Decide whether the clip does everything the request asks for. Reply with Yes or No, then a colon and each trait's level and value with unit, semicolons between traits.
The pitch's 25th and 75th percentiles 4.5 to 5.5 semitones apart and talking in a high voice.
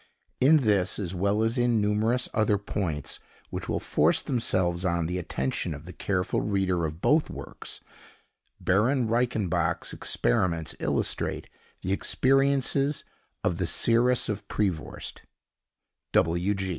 No: average, 5.2 semitones; low, 105 Hz